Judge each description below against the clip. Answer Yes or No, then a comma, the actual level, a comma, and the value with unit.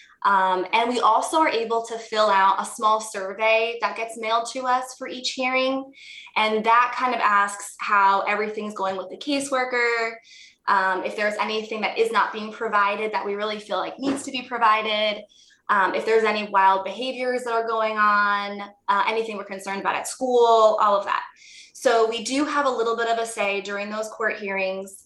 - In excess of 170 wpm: Yes, average, 200 wpm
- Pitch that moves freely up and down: No, average, 3.0 semitones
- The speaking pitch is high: Yes, high, 220 Hz